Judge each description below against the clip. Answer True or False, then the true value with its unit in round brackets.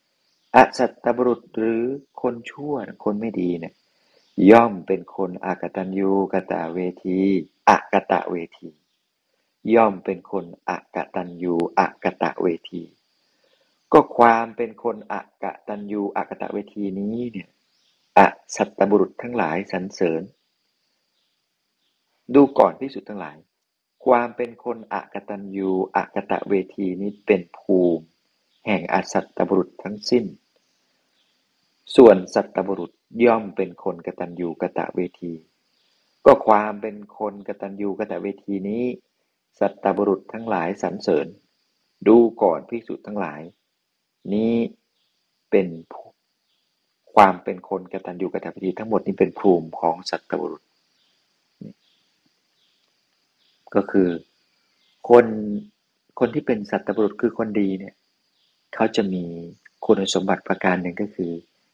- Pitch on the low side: True (100 Hz)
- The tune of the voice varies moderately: True (3.6 semitones)